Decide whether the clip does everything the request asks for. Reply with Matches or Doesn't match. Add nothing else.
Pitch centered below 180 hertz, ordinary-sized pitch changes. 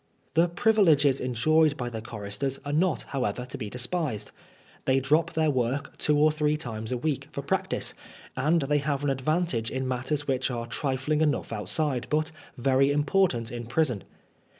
Matches